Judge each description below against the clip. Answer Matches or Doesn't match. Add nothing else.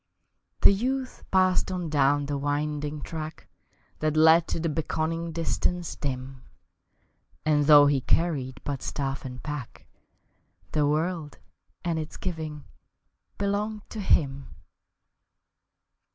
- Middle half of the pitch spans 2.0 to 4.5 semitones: Matches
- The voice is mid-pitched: Matches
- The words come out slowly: Matches